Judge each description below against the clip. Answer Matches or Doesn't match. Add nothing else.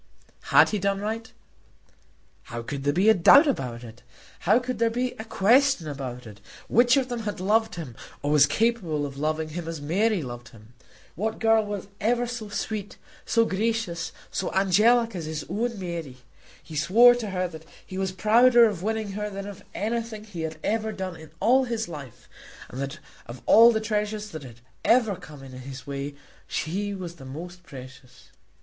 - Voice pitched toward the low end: Doesn't match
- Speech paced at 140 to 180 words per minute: Doesn't match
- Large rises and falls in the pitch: Matches